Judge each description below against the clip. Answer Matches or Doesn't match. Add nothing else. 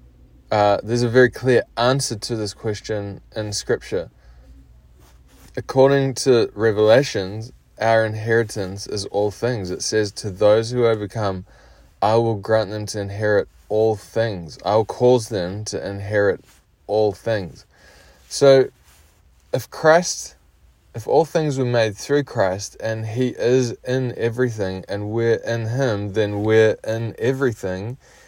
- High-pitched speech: Doesn't match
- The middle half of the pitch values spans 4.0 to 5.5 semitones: Doesn't match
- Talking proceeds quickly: Doesn't match